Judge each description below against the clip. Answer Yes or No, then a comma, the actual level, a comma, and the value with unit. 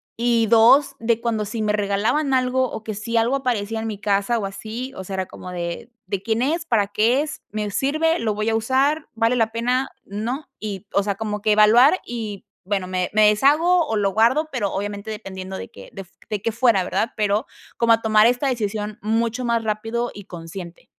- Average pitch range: Yes, average, 3.0 semitones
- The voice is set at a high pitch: Yes, high, 220 Hz